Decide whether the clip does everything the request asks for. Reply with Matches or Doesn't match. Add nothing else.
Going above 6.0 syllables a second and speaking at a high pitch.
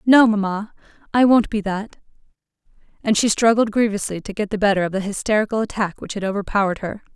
Matches